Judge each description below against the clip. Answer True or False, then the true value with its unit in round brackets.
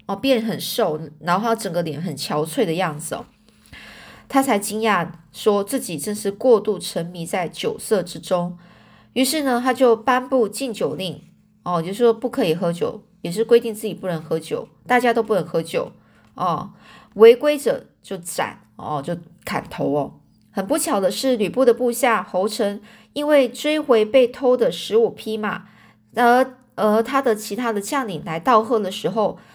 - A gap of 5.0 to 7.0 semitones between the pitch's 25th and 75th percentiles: True (5.5 semitones)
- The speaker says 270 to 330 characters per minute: False (245 characters per minute)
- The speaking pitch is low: False (215 Hz)